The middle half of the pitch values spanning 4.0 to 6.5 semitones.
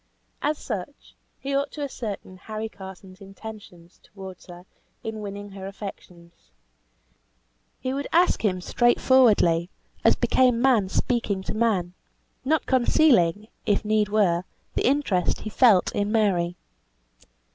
Yes: average, 4.5 semitones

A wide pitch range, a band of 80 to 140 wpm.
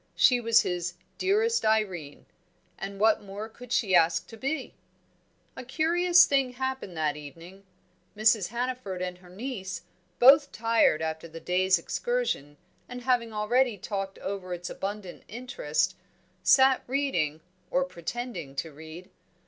Yes: wide, 6.3 semitones; slow, 135 wpm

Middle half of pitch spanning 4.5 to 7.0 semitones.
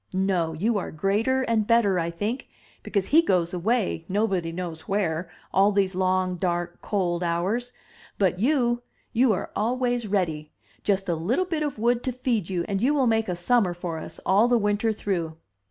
Yes: average, 5.0 semitones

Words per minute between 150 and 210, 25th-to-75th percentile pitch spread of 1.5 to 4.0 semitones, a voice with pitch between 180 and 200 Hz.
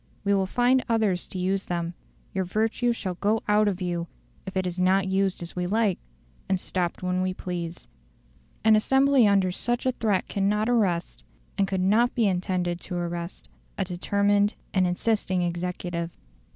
Yes: average, 170 wpm; average, 2.9 semitones; high, 190 Hz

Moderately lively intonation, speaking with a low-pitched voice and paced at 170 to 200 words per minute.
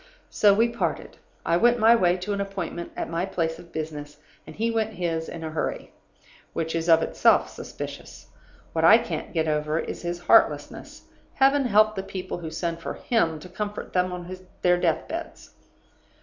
No: average, 4.5 semitones; medium, 180 Hz; average, 185 wpm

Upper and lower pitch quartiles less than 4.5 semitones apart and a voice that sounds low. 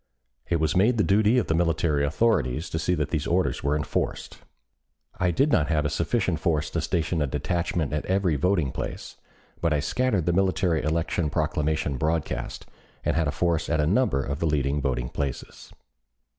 Yes: average, 3.4 semitones; very low, 80 Hz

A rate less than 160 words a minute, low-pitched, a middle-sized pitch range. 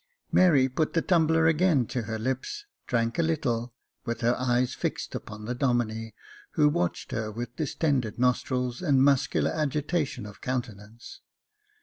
Yes: average, 145 wpm; low, 125 Hz; average, 4.5 semitones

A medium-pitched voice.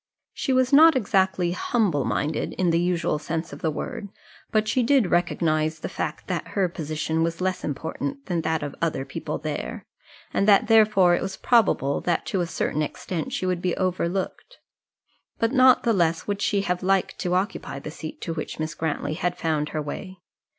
Yes: medium, 180 Hz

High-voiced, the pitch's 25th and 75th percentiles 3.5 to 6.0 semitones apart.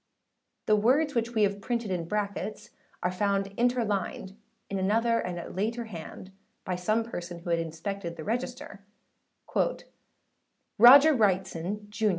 Yes: high, 205 Hz; average, 3.9 semitones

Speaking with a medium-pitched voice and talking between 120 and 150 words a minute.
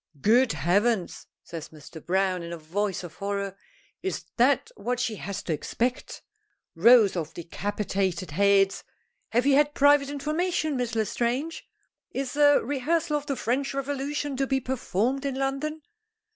No: high, 240 Hz; average, 145 wpm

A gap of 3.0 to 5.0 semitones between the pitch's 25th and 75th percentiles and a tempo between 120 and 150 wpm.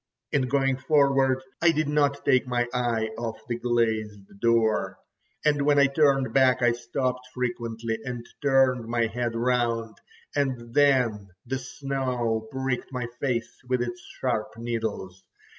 No: narrow, 2.5 semitones; average, 140 wpm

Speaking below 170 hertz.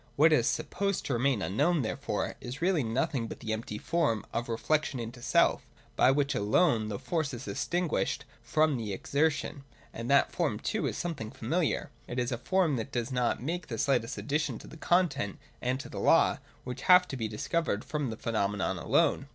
Yes: low, 135 Hz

